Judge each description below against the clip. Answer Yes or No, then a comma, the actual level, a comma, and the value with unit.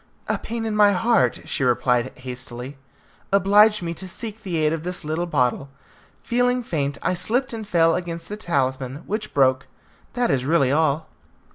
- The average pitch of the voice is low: No, medium, 170 Hz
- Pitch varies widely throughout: Yes, wide, 7.3 semitones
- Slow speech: No, average, 170 wpm